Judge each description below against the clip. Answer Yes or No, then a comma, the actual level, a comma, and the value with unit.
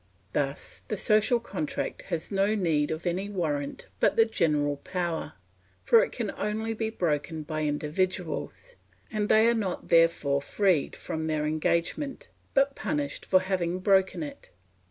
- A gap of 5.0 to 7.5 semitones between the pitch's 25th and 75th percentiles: Yes, wide, 5.5 semitones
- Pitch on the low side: No, medium, 180 Hz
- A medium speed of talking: Yes, average, 150 wpm